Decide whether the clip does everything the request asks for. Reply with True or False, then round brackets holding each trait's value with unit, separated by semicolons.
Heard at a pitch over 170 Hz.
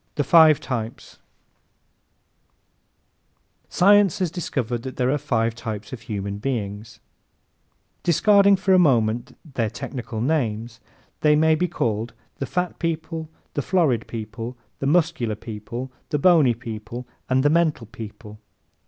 False (130 Hz)